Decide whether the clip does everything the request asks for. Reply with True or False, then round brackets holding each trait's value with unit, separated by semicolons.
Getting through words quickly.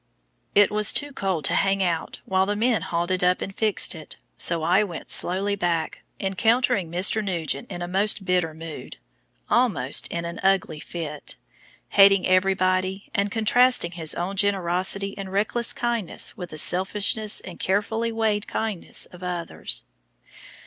False (155 wpm)